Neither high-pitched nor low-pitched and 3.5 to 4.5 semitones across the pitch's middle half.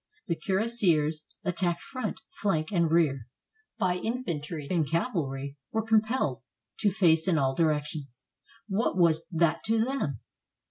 No: medium, 170 Hz; wide, 5.4 semitones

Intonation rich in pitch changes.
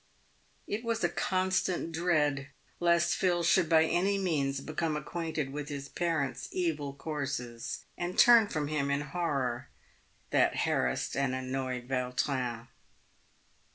No: average, 4.2 semitones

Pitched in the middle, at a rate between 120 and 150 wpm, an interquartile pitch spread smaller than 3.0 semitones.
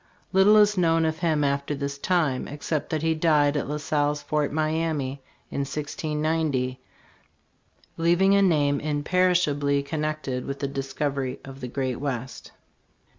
Yes: medium, 150 Hz; average, 145 wpm; narrow, 2.5 semitones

